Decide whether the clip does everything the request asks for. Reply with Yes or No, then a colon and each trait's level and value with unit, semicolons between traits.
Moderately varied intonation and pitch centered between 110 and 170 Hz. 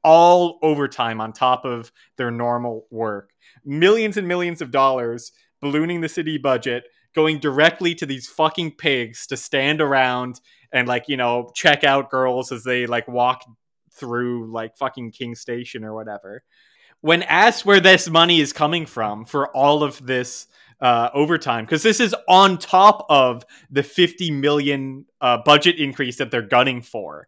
Yes: average, 4.6 semitones; low, 135 Hz